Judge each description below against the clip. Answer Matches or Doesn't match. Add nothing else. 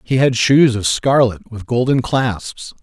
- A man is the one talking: Matches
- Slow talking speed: Doesn't match